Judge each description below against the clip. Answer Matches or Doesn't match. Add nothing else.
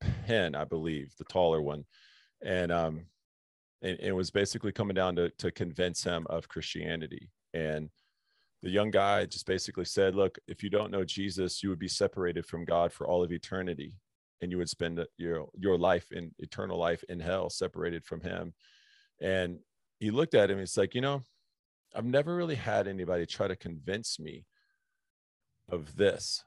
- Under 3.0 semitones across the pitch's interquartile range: Doesn't match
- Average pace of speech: Matches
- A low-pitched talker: Matches